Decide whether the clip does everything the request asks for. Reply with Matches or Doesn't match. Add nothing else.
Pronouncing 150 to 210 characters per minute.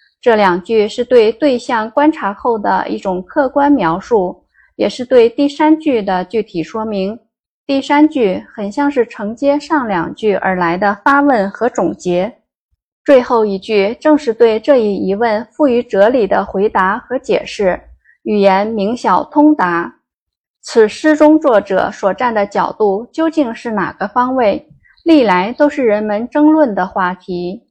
Doesn't match